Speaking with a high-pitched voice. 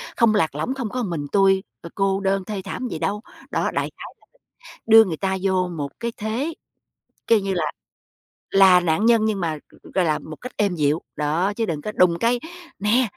Yes: high, 195 Hz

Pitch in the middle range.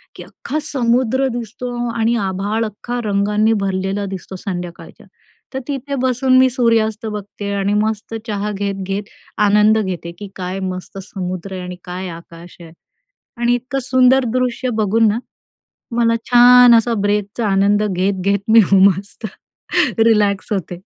No: high, 210 Hz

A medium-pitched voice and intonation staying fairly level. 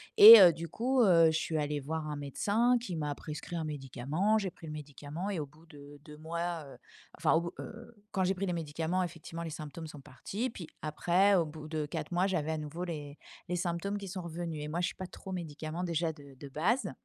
No: medium, 165 Hz; average, 3.3 semitones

